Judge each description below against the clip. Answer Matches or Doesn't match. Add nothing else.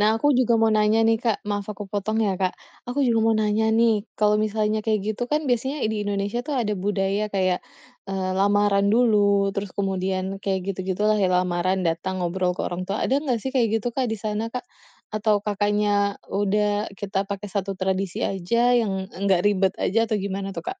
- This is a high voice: Matches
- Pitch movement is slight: Matches